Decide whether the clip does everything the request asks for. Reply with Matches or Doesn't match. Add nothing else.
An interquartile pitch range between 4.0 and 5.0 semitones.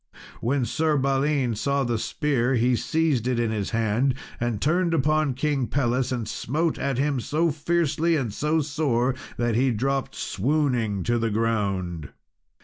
Matches